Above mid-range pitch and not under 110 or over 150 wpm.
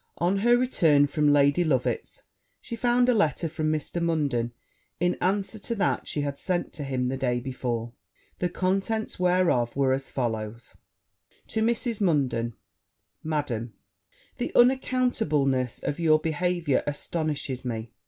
No: medium, 155 Hz; average, 140 wpm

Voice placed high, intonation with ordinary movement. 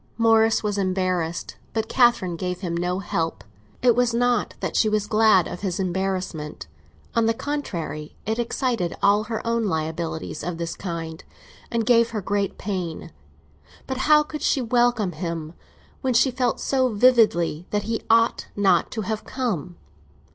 Yes: high, 205 Hz; average, 4.8 semitones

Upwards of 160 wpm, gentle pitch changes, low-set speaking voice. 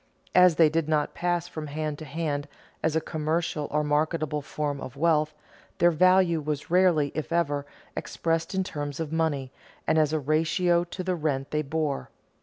No: average, 180 wpm; narrow, 2.2 semitones; medium, 155 Hz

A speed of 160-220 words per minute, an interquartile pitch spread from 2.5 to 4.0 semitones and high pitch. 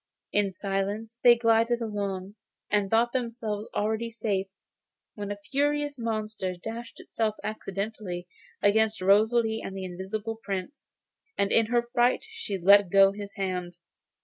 No: average, 140 wpm; average, 2.8 semitones; high, 215 Hz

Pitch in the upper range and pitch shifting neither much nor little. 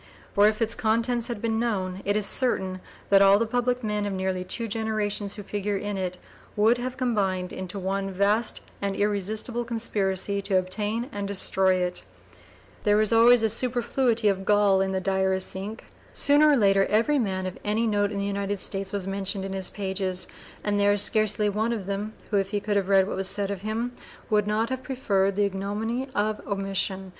No: high, 205 Hz; narrow, 2.3 semitones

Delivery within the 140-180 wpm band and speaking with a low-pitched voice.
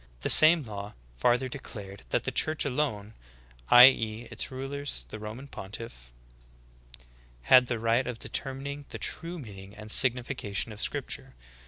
Yes: average, 145 wpm; low, 120 Hz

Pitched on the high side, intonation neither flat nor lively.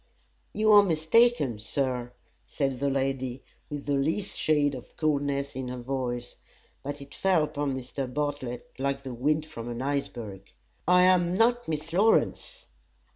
No: medium, 140 Hz; average, 3.6 semitones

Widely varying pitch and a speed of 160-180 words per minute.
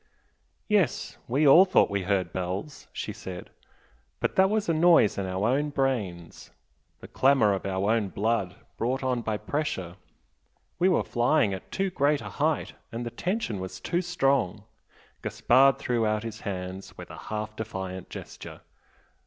Yes: wide, 6.8 semitones; average, 165 wpm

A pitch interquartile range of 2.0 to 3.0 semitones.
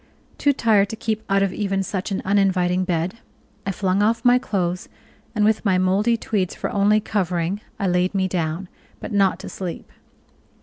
Yes: narrow, 2.4 semitones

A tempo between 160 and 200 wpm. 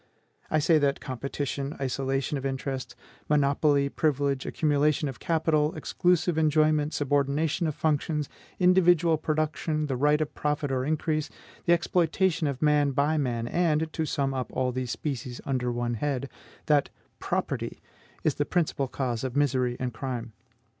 No: average, 145 wpm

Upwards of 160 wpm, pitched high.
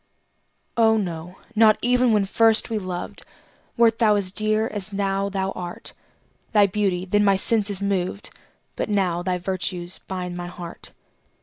No: average, 150 wpm; high, 195 Hz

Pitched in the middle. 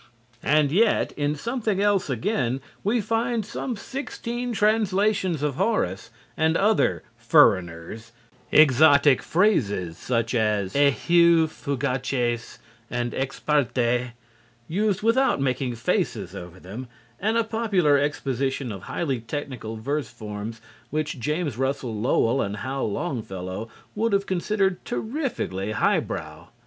Yes: medium, 145 Hz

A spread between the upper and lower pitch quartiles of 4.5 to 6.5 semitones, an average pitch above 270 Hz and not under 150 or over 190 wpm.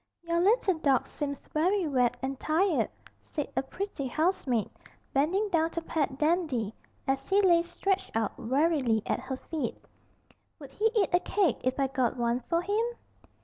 Yes: wide, 5.5 semitones; very high, 310 Hz; average, 165 wpm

